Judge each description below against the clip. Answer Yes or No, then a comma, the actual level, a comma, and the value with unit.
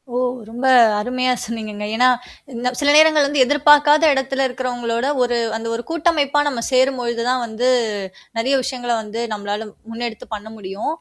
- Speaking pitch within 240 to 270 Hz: Yes, very high, 250 Hz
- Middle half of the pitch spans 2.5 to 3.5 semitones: Yes, average, 3.1 semitones